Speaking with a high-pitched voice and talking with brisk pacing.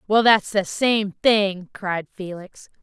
No: high, 200 Hz; average, 150 wpm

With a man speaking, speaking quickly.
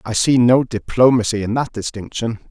No: male; average, 170 wpm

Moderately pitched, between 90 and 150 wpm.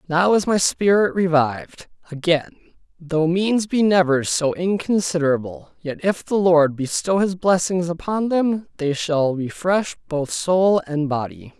Yes: medium, 170 Hz; average, 145 wpm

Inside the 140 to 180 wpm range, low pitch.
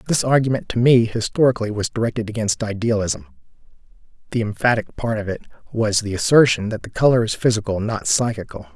Yes: average, 165 wpm; low, 115 Hz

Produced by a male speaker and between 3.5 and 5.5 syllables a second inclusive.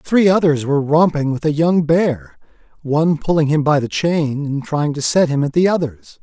Yes: male; 4.9 syllables/s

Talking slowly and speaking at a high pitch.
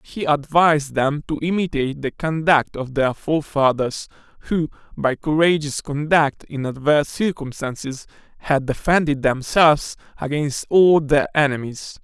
No: slow, 120 wpm; medium, 150 Hz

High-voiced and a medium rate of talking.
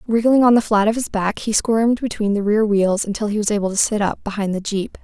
No: high, 210 Hz; fast, 275 wpm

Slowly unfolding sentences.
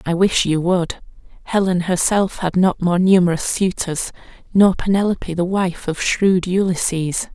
No: average, 145 wpm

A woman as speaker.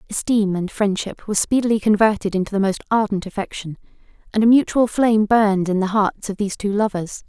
Yes: female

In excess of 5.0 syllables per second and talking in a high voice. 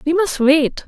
No: 4.1 syllables/s; very high, 310 Hz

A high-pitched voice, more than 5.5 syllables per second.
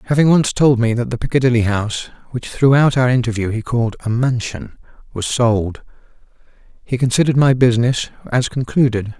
No: low, 120 Hz; 5.7 syllables/s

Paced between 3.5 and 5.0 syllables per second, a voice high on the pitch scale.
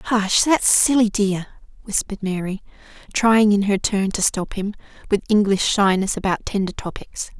Yes: 4.7 syllables/s; high, 205 Hz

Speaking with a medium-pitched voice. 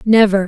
No: high, 205 Hz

